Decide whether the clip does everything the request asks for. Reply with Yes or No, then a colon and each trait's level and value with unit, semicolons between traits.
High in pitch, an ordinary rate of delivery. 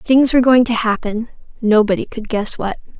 Yes: high, 225 Hz; average, 180 wpm